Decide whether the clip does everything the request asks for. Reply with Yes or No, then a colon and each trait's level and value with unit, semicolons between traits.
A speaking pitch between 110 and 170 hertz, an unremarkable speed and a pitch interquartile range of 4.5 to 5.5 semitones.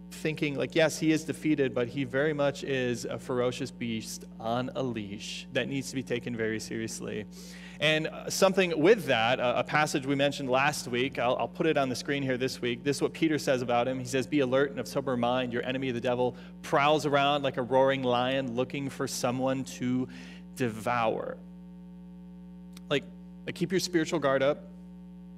Yes: medium, 140 Hz; average, 190 wpm; average, 4.8 semitones